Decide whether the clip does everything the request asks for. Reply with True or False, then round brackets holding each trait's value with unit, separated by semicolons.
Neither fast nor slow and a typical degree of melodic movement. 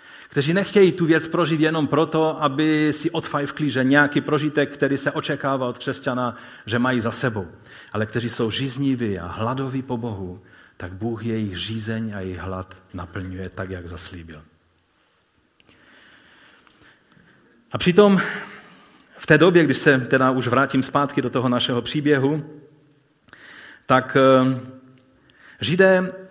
True (130 wpm; 4.9 semitones)